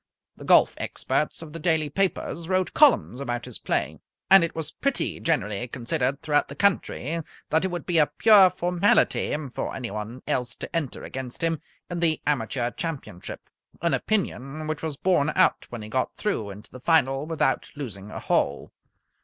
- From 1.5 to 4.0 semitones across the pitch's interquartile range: No, average, 5.2 semitones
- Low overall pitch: No, medium, 150 Hz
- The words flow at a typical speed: Yes, average, 175 wpm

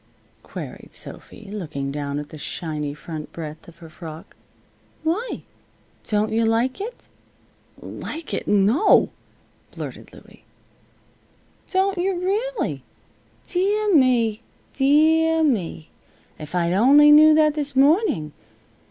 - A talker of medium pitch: No, very high, 255 Hz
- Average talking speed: No, slow, 115 wpm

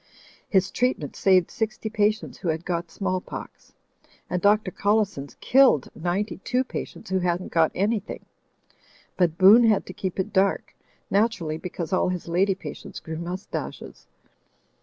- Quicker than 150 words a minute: No, average, 145 wpm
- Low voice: No, high, 190 Hz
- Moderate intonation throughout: Yes, average, 3.4 semitones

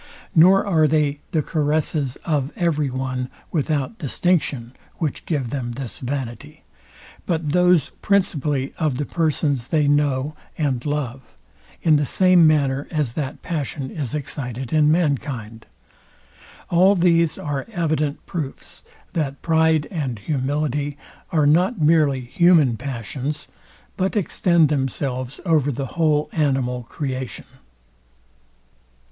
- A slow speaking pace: Yes, slow, 120 wpm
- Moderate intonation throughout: Yes, average, 3.3 semitones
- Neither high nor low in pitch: Yes, medium, 145 Hz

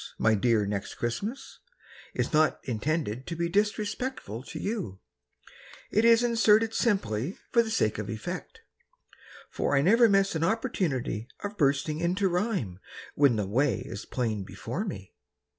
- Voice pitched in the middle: Yes, medium, 160 Hz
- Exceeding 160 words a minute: No, average, 145 wpm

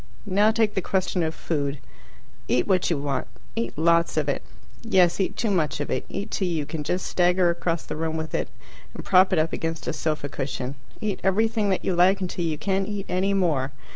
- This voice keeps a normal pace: No, fast, 215 wpm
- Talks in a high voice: No, medium, 175 Hz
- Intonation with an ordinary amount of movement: Yes, average, 3.7 semitones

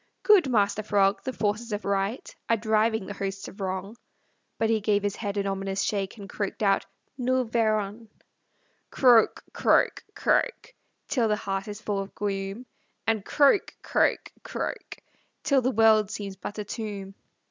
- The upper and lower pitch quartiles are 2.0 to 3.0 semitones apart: Yes, narrow, 2.4 semitones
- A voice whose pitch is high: Yes, high, 210 Hz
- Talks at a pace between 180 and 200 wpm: No, average, 160 wpm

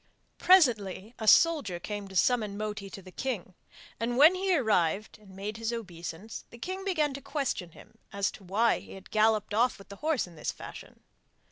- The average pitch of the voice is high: Yes, high, 215 Hz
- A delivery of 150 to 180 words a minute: No, average, 195 wpm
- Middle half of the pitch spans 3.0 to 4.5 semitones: No, average, 5.1 semitones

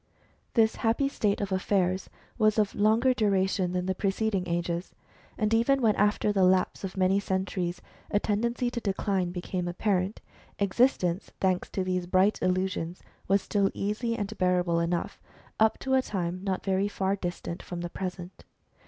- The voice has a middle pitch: No, high, 195 Hz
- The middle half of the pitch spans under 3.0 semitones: Yes, narrow, 2.6 semitones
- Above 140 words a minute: Yes, average, 160 wpm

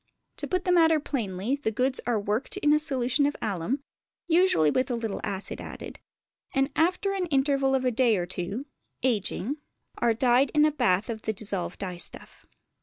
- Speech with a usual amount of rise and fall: No, wide, 5.7 semitones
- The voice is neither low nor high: No, very high, 255 Hz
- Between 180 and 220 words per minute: Yes, average, 185 wpm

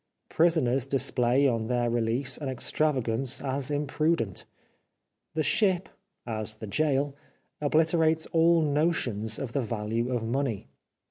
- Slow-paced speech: Yes, slow, 120 wpm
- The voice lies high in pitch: No, low, 135 Hz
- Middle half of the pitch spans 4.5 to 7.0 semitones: Yes, average, 4.8 semitones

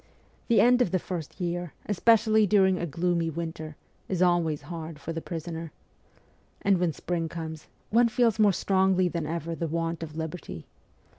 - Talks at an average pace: Yes, average, 165 wpm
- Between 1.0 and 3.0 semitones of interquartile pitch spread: Yes, average, 2.7 semitones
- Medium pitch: Yes, medium, 170 Hz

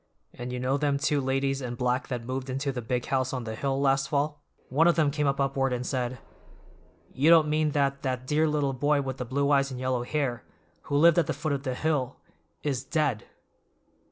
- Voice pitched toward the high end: No, low, 135 Hz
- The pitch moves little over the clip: Yes, narrow, 2.3 semitones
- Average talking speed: No, fast, 220 wpm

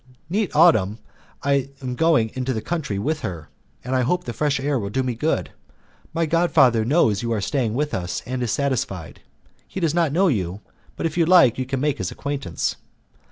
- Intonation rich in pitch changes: Yes, wide, 5.9 semitones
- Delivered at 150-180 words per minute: No, fast, 205 wpm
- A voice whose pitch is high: No, low, 130 Hz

